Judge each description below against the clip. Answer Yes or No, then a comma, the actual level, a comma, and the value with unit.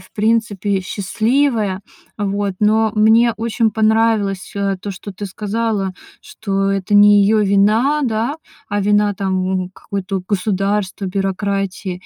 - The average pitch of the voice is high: Yes, high, 205 Hz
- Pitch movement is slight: Yes, narrow, 2.0 semitones